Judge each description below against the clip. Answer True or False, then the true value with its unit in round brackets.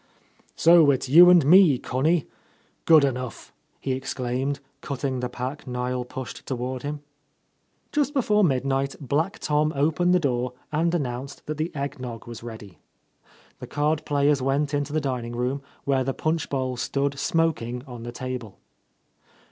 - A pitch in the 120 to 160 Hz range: True (140 Hz)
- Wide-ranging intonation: False (3.4 semitones)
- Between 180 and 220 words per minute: False (155 wpm)